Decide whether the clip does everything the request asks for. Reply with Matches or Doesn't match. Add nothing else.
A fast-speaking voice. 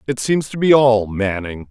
Matches